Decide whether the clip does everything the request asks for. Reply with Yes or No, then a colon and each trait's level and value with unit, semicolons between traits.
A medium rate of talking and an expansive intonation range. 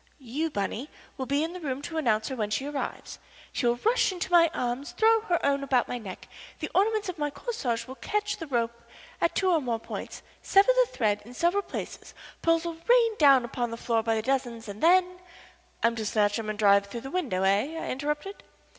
No: fast, 220 wpm; wide, 7.0 semitones